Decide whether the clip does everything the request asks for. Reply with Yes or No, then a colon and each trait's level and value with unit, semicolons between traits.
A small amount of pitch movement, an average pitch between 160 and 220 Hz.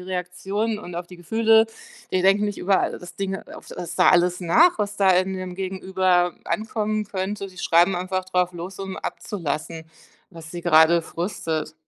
Yes: narrow, 2.1 semitones; medium, 185 Hz